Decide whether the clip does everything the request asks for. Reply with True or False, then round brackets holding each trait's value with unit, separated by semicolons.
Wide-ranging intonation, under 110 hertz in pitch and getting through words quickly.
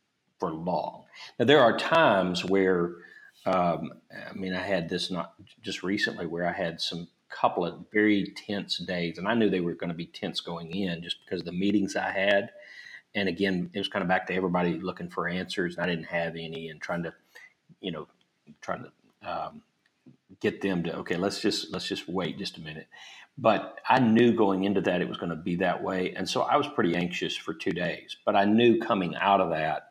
False (2.5 semitones; 90 Hz; 220 wpm)